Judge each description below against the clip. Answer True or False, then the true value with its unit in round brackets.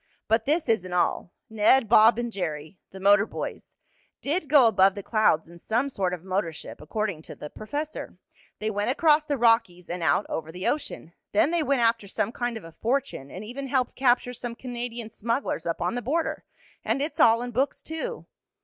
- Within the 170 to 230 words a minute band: True (200 wpm)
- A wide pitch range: True (5.7 semitones)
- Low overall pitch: False (225 Hz)